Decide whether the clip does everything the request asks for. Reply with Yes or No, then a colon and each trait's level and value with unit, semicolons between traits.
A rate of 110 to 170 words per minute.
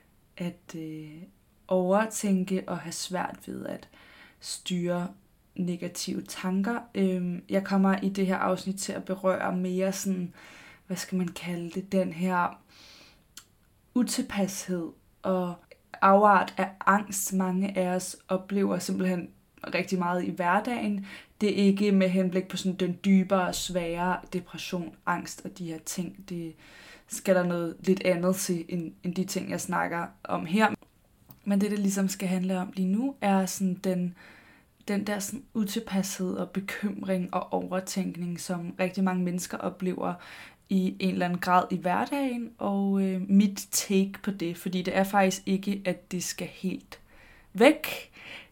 Yes: average, 150 wpm